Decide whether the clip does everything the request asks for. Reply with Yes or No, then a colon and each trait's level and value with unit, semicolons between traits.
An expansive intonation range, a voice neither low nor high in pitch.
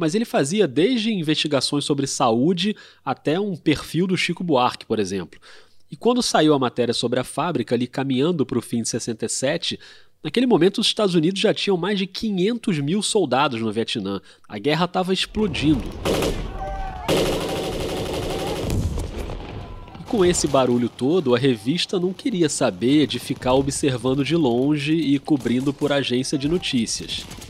Yes: wide, 6.9 semitones; medium, 145 Hz